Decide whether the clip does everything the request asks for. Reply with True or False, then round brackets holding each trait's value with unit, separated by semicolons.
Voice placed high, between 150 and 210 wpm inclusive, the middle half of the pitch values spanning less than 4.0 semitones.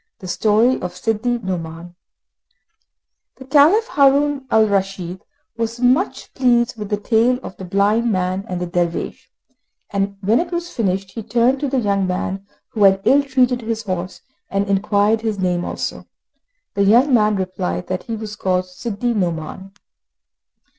False (210 Hz; 160 wpm; 4.4 semitones)